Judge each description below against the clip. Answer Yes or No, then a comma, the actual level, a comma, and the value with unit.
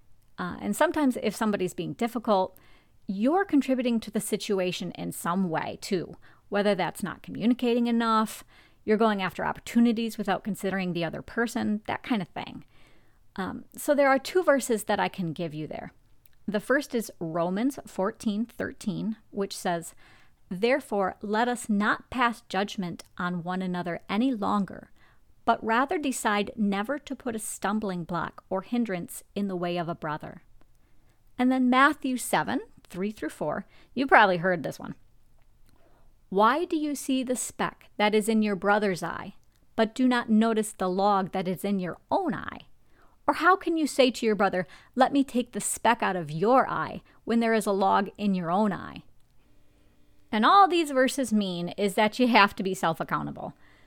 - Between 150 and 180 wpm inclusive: Yes, average, 175 wpm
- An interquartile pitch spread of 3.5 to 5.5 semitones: Yes, average, 4.6 semitones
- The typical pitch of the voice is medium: No, high, 210 Hz